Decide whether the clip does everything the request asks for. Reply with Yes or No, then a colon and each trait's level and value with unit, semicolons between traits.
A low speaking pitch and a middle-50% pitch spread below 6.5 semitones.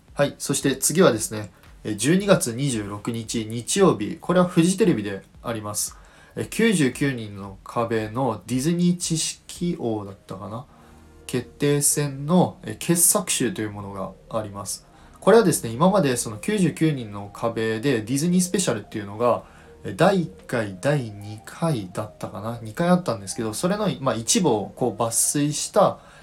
No: low, 120 Hz; wide, 7.1 semitones